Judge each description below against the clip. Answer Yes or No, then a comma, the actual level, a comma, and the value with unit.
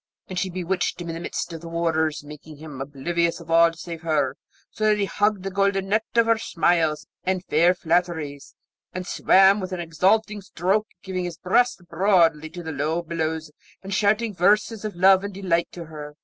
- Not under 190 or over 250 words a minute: Yes, average, 195 wpm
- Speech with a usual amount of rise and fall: Yes, average, 3.3 semitones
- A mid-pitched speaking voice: Yes, medium, 175 Hz